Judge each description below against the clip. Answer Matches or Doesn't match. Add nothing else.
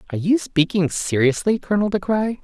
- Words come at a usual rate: Matches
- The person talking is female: Matches